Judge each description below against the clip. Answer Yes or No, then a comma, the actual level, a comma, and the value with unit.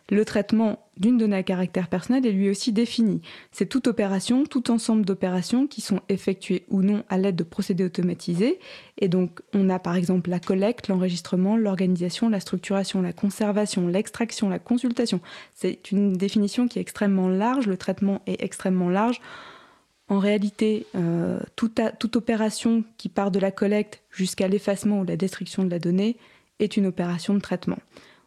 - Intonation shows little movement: No, average, 3.0 semitones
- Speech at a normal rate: Yes, average, 170 wpm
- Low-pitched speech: No, high, 200 Hz